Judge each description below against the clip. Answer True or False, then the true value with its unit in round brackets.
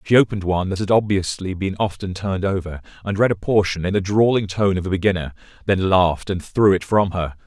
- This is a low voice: True (95 Hz)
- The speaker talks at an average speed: False (225 wpm)